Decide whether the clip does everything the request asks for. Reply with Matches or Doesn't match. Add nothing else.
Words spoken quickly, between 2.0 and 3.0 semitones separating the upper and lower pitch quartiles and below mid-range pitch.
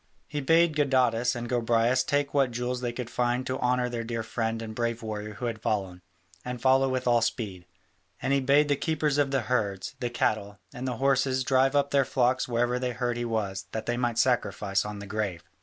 Matches